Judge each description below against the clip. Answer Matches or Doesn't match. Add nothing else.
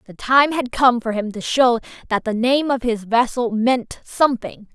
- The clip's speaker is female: Matches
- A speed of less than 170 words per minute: Doesn't match